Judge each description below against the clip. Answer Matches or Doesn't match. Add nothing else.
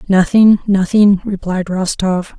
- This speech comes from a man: Doesn't match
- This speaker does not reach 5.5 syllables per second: Matches